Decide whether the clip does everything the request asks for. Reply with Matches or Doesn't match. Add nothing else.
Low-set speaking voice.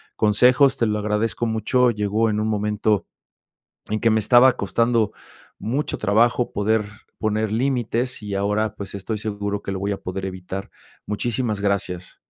Matches